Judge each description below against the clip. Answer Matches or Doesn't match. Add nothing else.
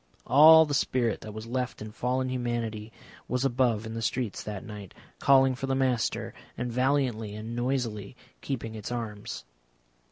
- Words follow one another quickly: Doesn't match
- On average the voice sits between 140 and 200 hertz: Doesn't match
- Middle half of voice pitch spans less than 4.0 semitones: Matches